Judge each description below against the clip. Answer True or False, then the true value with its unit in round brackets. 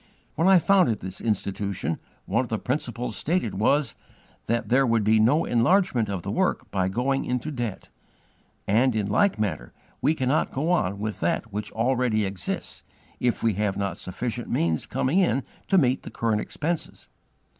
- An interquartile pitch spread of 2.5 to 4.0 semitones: False (4.6 semitones)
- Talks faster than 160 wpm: True (170 wpm)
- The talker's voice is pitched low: True (115 Hz)